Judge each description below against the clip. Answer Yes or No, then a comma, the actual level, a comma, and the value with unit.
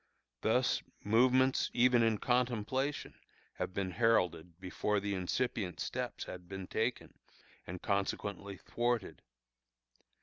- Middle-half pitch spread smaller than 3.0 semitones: No, average, 4.6 semitones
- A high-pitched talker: No, low, 105 Hz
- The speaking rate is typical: No, slow, 105 wpm